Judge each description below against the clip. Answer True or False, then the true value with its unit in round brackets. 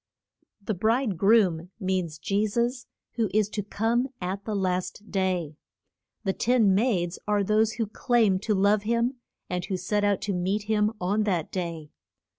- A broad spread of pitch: False (2.9 semitones)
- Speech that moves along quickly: False (165 wpm)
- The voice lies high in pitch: True (205 Hz)